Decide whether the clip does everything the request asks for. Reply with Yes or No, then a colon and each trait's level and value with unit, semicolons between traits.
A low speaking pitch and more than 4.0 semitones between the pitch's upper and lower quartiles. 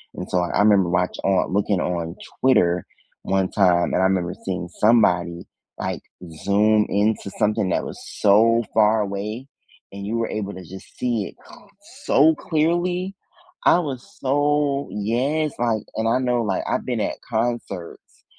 Yes: low, 105 Hz; average, 4.4 semitones